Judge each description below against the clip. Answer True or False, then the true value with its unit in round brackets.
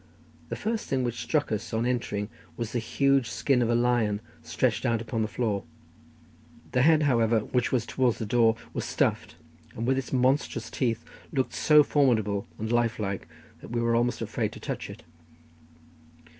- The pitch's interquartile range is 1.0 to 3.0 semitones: True (2.7 semitones)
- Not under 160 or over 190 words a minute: True (175 wpm)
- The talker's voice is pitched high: False (120 Hz)